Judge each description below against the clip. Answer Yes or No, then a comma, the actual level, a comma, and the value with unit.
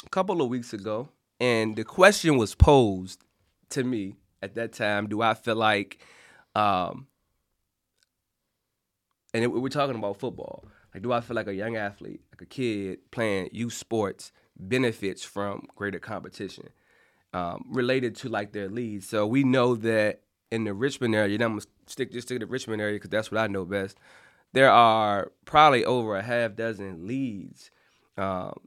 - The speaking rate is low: No, average, 175 wpm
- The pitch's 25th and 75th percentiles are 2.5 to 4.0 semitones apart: Yes, average, 3.2 semitones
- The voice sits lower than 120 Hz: Yes, low, 110 Hz